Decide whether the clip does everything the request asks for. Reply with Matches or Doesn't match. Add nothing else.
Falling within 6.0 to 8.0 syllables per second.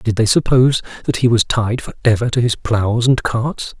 Doesn't match